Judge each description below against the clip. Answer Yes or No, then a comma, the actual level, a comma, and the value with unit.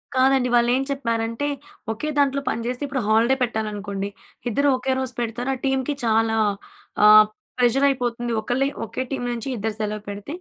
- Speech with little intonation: No, average, 3.2 semitones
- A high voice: Yes, high, 240 Hz